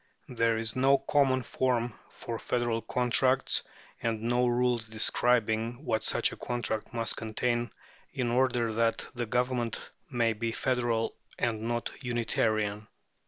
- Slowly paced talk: Yes, slow, 130 wpm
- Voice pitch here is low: Yes, low, 120 Hz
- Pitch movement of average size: No, narrow, 1.6 semitones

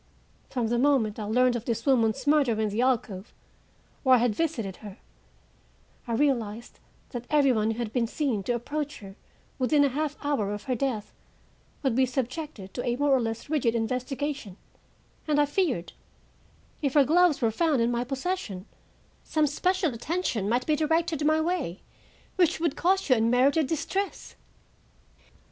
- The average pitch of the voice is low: No, very high, 255 Hz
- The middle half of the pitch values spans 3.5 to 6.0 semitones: Yes, average, 4.7 semitones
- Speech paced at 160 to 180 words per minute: Yes, average, 165 wpm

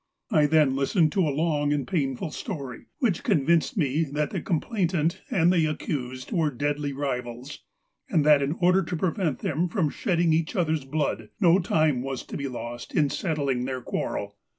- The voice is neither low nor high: Yes, medium, 150 Hz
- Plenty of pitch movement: No, average, 3.9 semitones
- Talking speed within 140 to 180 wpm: Yes, average, 175 wpm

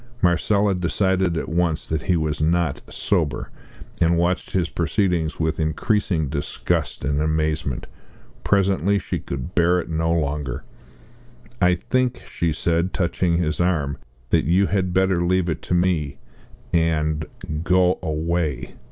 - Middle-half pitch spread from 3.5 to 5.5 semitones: No, average, 2.8 semitones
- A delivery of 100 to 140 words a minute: Yes, slow, 135 wpm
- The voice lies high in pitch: No, very low, 85 Hz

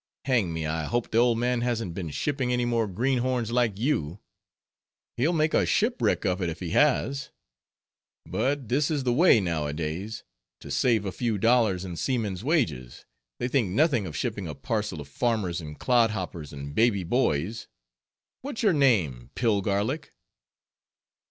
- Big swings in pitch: Yes, wide, 6.1 semitones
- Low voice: Yes, low, 115 Hz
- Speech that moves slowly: No, average, 155 wpm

